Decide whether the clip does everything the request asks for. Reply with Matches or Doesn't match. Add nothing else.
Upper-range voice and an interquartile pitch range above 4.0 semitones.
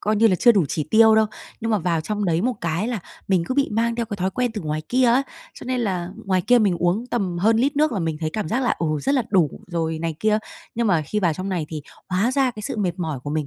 Matches